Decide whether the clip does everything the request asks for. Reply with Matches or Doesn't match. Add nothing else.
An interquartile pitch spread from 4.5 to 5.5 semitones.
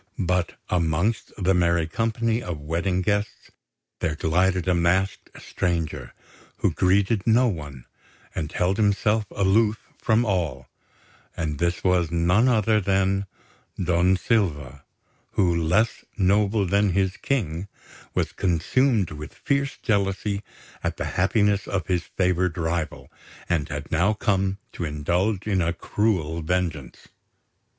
Doesn't match